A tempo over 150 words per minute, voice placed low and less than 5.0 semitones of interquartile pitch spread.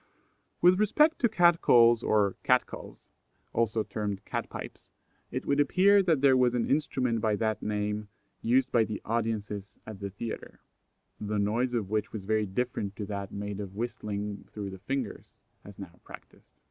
Yes: average, 170 wpm; low, 110 Hz; average, 3.7 semitones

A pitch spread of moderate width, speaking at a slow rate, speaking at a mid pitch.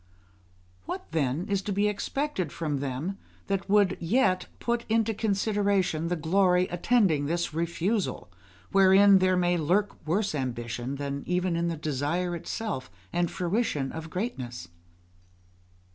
Yes: average, 4.4 semitones; slow, 130 wpm; medium, 180 Hz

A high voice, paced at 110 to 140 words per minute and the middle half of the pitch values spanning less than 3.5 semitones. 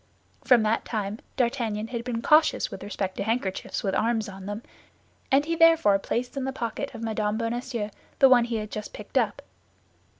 No: high, 230 Hz; average, 190 wpm; average, 3.0 semitones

